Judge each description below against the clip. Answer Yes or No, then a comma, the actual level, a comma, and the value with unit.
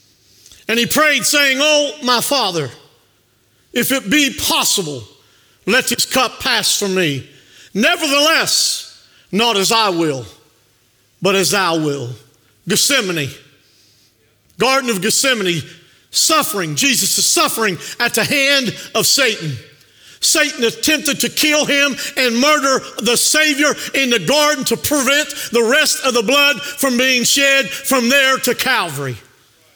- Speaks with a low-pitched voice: No, high, 230 Hz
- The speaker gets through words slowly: Yes, slow, 130 wpm